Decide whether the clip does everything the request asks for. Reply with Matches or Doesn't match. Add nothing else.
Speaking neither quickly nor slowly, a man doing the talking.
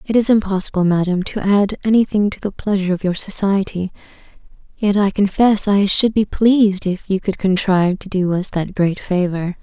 Doesn't match